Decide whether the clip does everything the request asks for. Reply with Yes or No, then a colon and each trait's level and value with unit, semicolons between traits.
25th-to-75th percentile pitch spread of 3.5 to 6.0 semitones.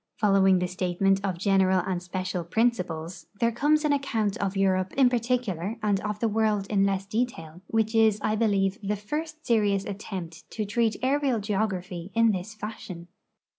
No: average, 3.1 semitones